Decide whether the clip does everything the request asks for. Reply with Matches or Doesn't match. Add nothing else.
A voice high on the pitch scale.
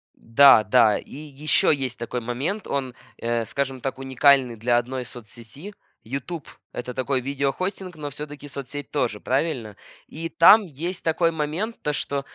Doesn't match